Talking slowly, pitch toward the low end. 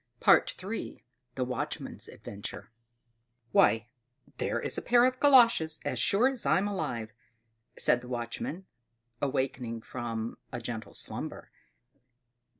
Yes: slow, 115 wpm; low, 130 Hz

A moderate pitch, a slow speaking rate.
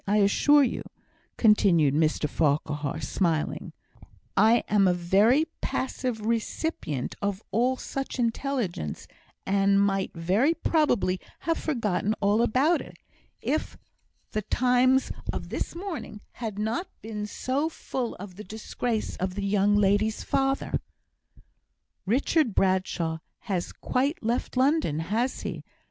No: high, 215 Hz; slow, 125 wpm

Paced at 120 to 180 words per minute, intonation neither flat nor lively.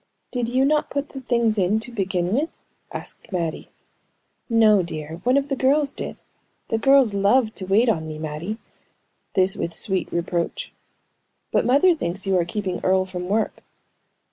No: average, 170 wpm; wide, 5.9 semitones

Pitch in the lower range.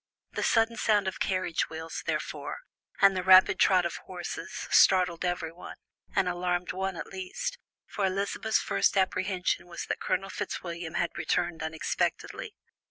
No: medium, 185 Hz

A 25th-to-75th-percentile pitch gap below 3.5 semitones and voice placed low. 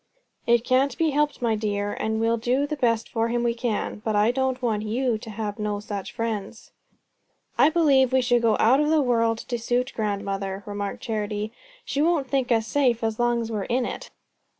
No: average, 3.0 semitones; high, 230 Hz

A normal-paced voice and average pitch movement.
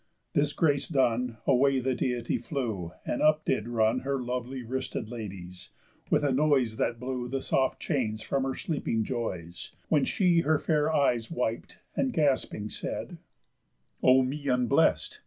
Yes: average, 155 wpm; average, 3.5 semitones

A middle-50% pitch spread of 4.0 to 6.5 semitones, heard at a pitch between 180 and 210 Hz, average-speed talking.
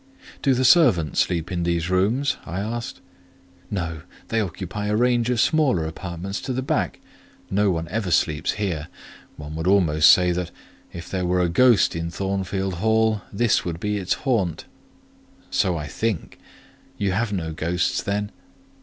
No: average, 4.6 semitones; very low, 95 Hz; average, 165 wpm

